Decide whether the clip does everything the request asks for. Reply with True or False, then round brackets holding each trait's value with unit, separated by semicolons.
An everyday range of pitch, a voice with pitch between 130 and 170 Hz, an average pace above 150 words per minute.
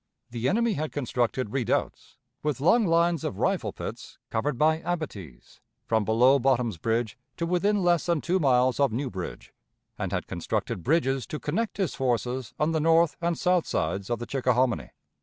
False (5.9 semitones; 135 Hz; 175 wpm)